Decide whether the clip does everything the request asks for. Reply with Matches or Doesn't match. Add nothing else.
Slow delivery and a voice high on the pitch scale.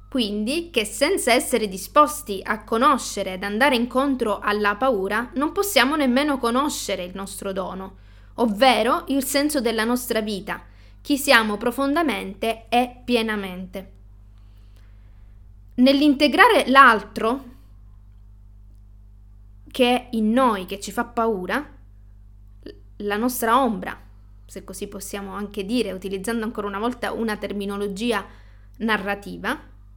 Matches